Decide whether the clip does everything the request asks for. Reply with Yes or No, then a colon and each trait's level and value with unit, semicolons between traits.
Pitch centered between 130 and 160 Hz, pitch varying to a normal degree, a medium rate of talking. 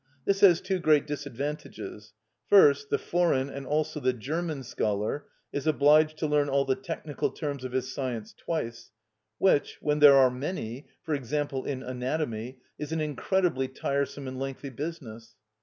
Yes: medium, 140 Hz; average, 3.0 semitones; average, 150 wpm